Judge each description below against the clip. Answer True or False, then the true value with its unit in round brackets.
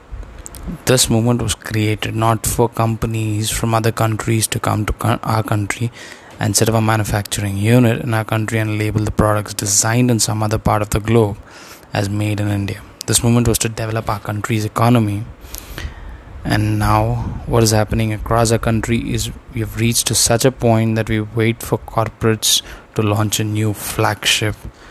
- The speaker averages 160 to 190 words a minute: True (180 wpm)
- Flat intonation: True (1.4 semitones)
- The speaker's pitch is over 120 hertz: False (110 Hz)